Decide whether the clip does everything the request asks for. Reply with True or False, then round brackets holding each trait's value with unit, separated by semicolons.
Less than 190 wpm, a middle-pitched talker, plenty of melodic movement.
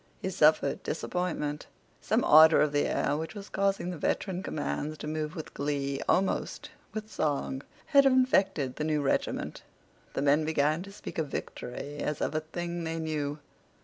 False (160 wpm; 155 Hz; 3.6 semitones)